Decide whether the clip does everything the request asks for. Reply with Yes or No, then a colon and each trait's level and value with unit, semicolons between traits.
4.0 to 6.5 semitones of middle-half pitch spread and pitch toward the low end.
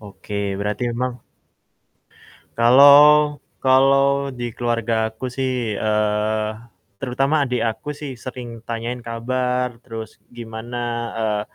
No: average, 2.9 semitones; low, 120 Hz